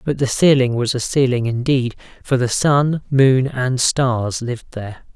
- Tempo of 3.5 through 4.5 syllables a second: Yes, 4.3 syllables/s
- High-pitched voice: No, low, 130 Hz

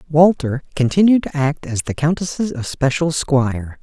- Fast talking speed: No, average, 140 wpm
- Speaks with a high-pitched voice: No, medium, 150 Hz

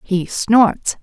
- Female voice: Yes, female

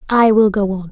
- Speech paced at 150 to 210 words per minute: No, fast, 265 wpm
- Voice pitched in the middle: No, high, 205 Hz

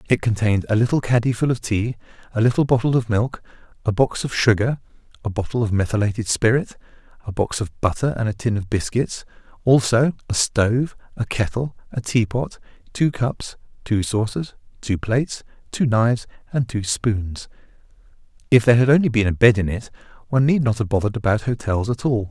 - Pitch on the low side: Yes, low, 115 Hz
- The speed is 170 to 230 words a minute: Yes, average, 180 wpm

